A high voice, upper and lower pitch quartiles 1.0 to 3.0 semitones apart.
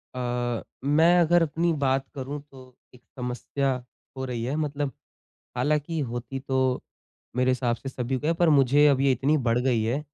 No: low, 135 Hz; average, 2.7 semitones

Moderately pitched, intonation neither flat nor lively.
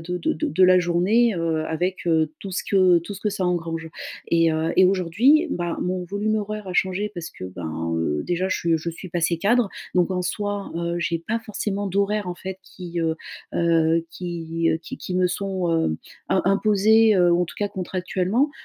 Yes: medium, 180 Hz; average, 3.0 semitones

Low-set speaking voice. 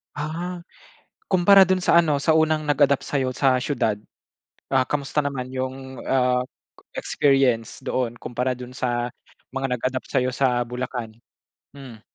Yes: low, 130 Hz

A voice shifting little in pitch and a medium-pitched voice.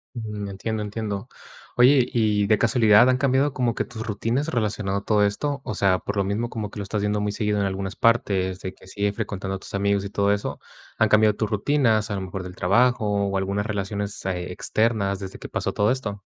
No: narrow, 2.3 semitones; low, 105 Hz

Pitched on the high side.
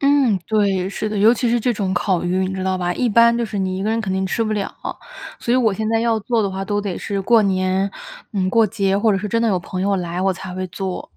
Yes: high, 200 Hz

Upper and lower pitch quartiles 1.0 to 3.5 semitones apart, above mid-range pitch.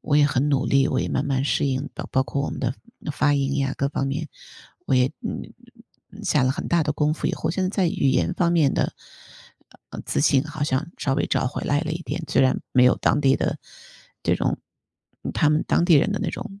No: average, 3.0 semitones; medium, 145 Hz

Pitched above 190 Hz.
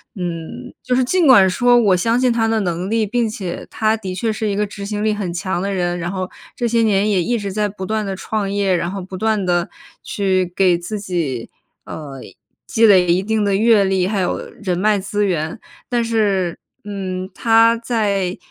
Yes: high, 200 Hz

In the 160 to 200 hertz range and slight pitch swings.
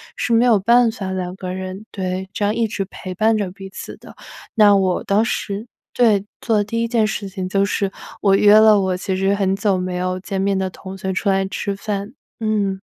Yes: high, 195 Hz; narrow, 2.1 semitones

